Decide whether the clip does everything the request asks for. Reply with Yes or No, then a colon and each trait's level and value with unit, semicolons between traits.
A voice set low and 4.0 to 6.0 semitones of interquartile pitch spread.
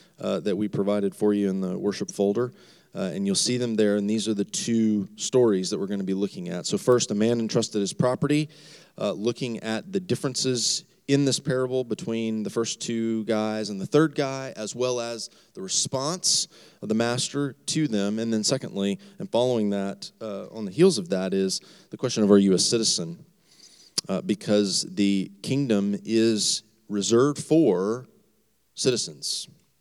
Yes: low, 115 Hz; average, 5.3 semitones